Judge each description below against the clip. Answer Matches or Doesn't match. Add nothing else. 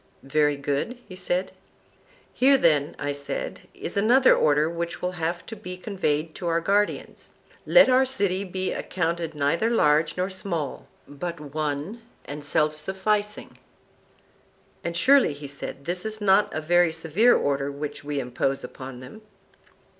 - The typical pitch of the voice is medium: Matches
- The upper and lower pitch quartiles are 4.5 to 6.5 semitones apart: Matches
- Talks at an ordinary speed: Matches